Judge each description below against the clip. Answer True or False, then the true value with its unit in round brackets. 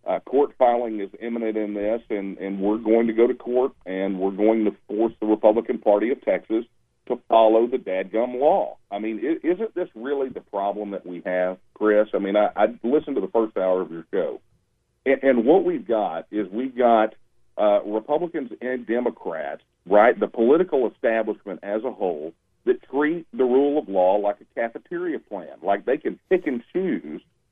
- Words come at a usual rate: True (190 wpm)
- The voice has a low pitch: True (110 Hz)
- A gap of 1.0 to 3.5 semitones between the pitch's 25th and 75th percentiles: False (4.0 semitones)